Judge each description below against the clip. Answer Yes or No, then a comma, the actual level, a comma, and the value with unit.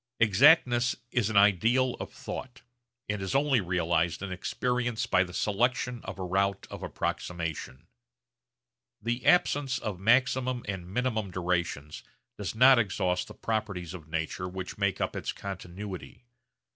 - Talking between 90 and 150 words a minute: Yes, average, 140 wpm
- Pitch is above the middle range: No, low, 100 Hz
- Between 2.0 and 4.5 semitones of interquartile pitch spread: No, average, 5.2 semitones